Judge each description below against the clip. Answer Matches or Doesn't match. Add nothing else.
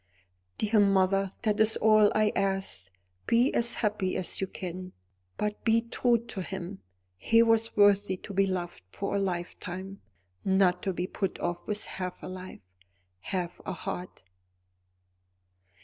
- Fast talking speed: Doesn't match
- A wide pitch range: Doesn't match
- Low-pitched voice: Doesn't match